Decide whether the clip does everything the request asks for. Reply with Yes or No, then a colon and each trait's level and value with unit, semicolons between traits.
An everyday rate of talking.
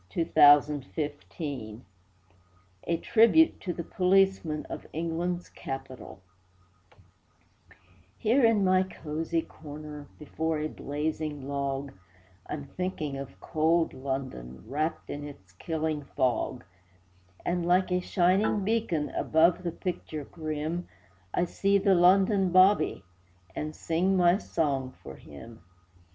No: slow, 115 wpm